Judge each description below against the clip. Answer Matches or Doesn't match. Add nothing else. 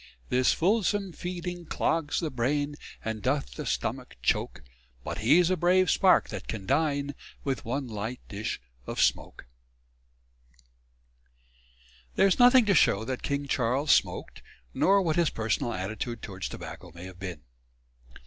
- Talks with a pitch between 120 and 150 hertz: Matches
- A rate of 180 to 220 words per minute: Doesn't match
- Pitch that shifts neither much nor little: Doesn't match